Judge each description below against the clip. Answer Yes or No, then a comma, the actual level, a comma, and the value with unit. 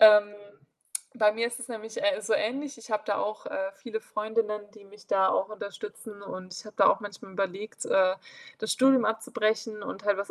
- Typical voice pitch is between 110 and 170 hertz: No, high, 215 Hz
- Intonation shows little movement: Yes, narrow, 1.8 semitones